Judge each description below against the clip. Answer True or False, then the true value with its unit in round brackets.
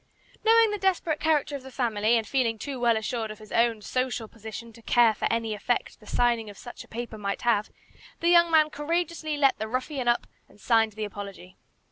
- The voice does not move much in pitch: False (4.8 semitones)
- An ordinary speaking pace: False (210 wpm)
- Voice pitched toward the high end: True (240 Hz)